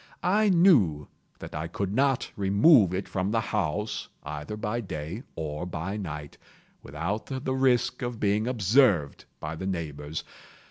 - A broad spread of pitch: Yes, wide, 7.3 semitones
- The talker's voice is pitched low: Yes, low, 100 Hz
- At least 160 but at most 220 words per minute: No, average, 145 wpm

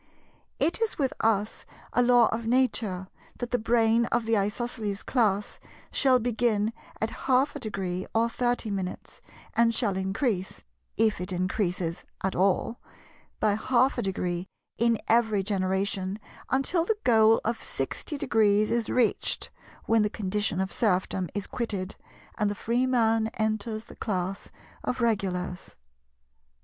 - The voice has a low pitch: No, high, 220 Hz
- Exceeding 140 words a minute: No, slow, 135 wpm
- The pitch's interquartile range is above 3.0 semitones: Yes, average, 3.5 semitones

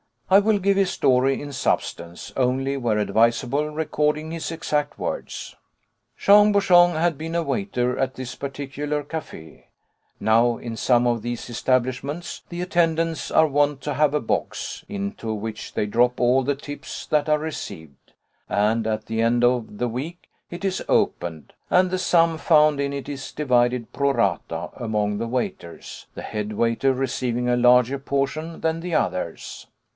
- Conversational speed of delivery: Yes, average, 160 wpm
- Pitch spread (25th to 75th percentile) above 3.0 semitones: Yes, average, 5.0 semitones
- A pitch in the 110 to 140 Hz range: Yes, low, 135 Hz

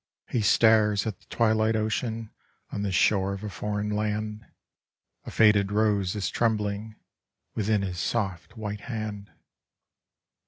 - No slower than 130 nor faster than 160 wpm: Yes, average, 140 wpm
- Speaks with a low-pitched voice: Yes, low, 105 Hz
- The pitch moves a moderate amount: No, narrow, 1.5 semitones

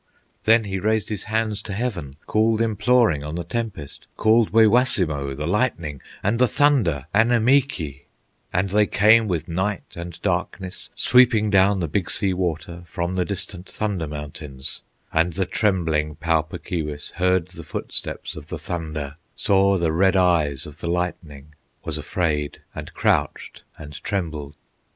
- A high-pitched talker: No, very low, 90 Hz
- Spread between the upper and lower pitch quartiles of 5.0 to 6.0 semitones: Yes, wide, 5.4 semitones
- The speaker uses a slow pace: No, average, 150 wpm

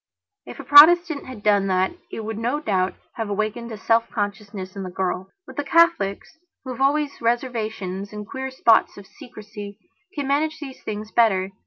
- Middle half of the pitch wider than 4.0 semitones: Yes, average, 4.9 semitones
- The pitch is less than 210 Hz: No, high, 220 Hz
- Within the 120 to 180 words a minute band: Yes, average, 175 wpm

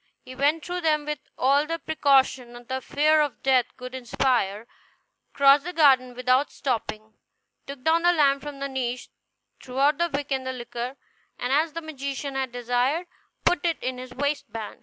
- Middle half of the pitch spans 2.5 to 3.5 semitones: Yes, average, 2.9 semitones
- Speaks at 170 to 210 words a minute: Yes, average, 180 wpm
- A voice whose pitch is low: No, very high, 275 Hz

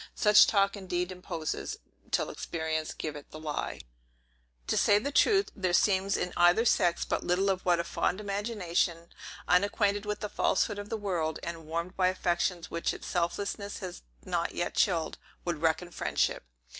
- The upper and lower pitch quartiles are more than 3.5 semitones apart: No, average, 3.2 semitones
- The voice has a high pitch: No, medium, 180 Hz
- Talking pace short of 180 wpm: Yes, average, 170 wpm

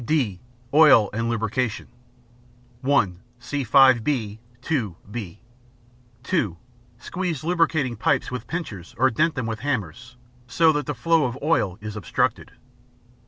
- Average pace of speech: No, slow, 130 wpm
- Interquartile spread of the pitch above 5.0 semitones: Yes, wide, 5.4 semitones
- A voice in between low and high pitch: No, low, 125 Hz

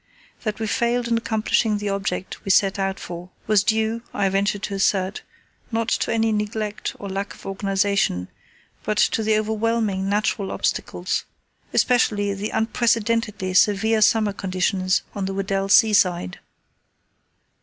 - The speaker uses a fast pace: No, average, 145 wpm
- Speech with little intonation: Yes, narrow, 2.1 semitones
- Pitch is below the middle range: No, high, 205 Hz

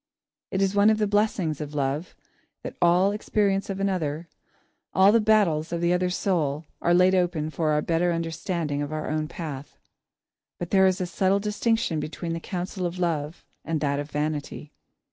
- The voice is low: No, medium, 175 Hz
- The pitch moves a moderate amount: Yes, average, 3.8 semitones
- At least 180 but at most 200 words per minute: Yes, average, 185 wpm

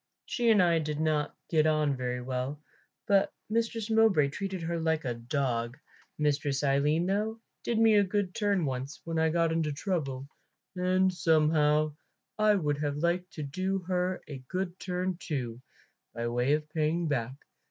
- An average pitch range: Yes, average, 4.6 semitones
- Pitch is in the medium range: Yes, medium, 160 Hz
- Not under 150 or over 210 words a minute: Yes, average, 165 wpm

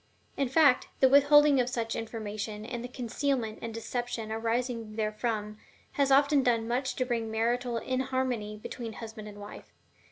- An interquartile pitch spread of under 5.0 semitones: Yes, average, 2.7 semitones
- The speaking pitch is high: Yes, high, 235 Hz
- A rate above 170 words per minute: No, average, 155 wpm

